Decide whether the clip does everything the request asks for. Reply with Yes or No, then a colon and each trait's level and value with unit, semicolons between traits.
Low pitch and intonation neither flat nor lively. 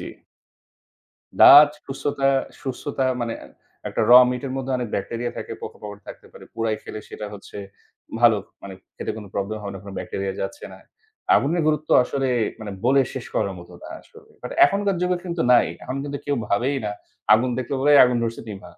Yes: low, 125 Hz; average, 4.9 semitones